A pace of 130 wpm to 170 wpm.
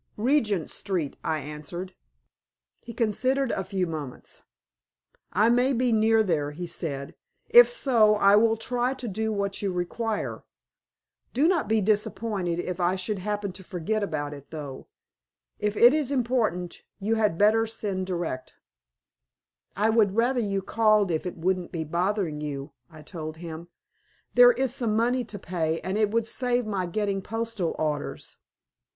Yes: average, 155 wpm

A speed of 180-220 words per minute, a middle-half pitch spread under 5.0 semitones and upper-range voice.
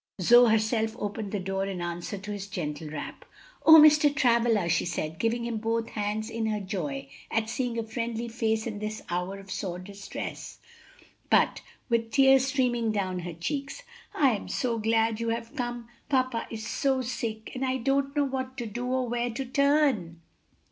Yes: average, 185 wpm; average, 3.8 semitones; high, 225 Hz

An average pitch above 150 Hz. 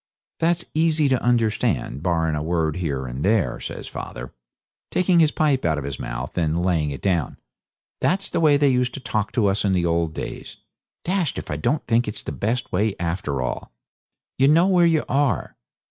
No: low, 105 Hz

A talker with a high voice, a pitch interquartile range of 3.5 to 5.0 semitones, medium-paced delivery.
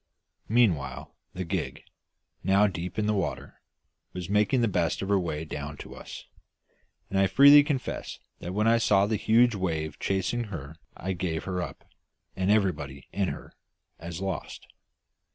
No: very low, 95 Hz; average, 4.1 semitones; average, 160 wpm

